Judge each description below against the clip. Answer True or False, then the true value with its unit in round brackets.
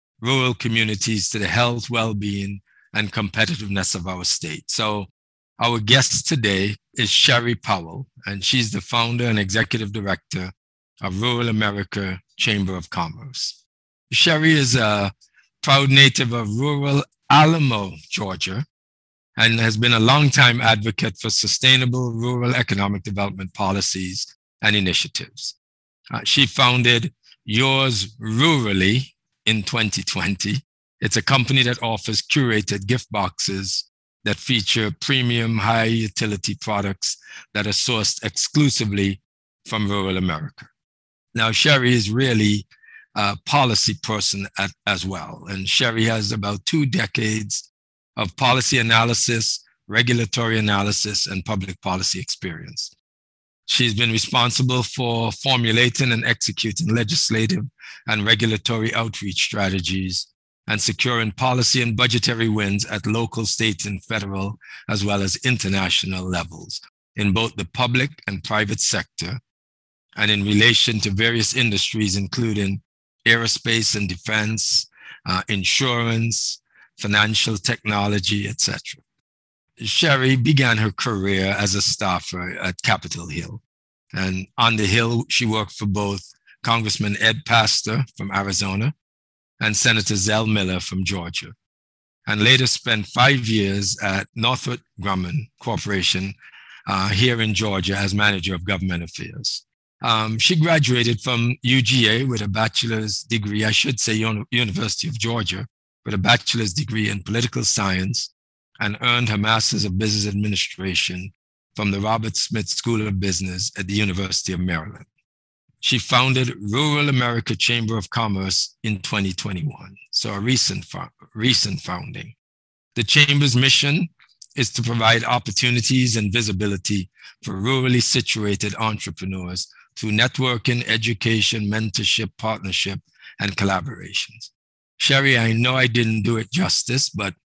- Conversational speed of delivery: False (125 wpm)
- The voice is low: True (110 Hz)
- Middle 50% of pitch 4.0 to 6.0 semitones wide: False (3.6 semitones)